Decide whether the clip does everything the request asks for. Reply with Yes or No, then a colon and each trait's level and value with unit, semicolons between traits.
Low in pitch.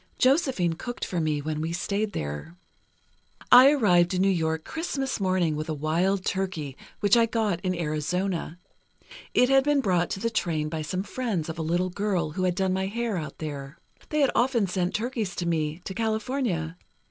No: medium, 185 Hz